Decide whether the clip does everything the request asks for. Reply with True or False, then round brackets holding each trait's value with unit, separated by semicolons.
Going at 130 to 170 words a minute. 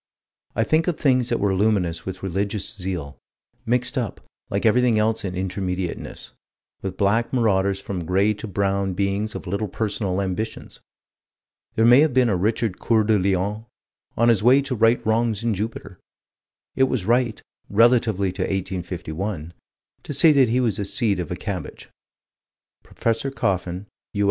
True (165 wpm)